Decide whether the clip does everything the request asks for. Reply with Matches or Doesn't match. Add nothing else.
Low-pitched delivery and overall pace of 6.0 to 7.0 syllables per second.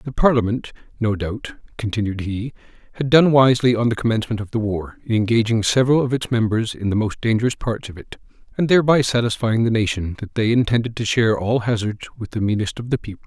Matches